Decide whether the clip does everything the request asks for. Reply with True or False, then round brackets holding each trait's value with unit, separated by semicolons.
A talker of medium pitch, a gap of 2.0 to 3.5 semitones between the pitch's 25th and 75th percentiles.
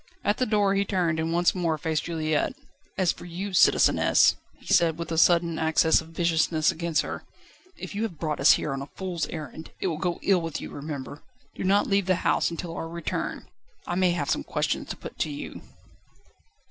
True (165 Hz; 2.4 semitones)